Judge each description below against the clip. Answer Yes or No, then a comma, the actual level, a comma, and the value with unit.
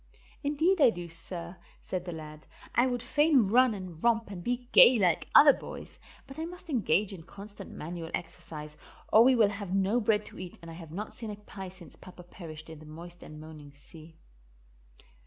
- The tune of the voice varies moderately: No, wide, 6.1 semitones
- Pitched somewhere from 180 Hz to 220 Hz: Yes, high, 190 Hz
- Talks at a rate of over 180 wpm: Yes, average, 200 wpm